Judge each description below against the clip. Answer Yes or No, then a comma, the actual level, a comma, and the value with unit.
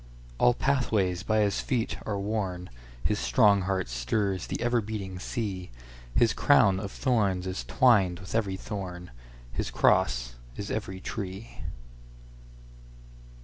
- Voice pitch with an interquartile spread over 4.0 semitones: No, average, 3.5 semitones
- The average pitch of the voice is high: No, very low, 95 Hz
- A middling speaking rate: No, slow, 115 wpm